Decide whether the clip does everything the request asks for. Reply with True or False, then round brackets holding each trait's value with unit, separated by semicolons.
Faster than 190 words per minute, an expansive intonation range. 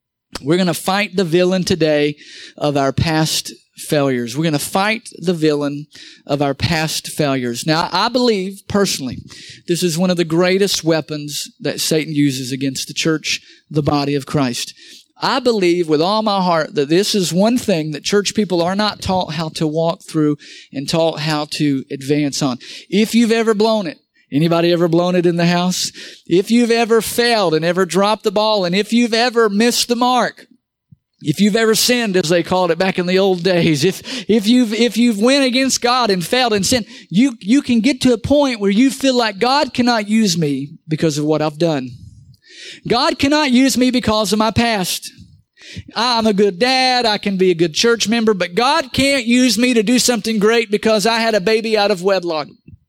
True (200 wpm; 6.5 semitones)